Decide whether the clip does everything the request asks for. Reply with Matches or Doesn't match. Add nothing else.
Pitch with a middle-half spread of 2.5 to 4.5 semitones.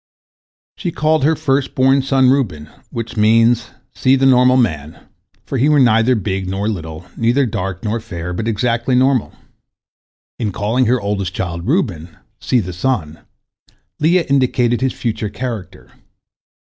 Doesn't match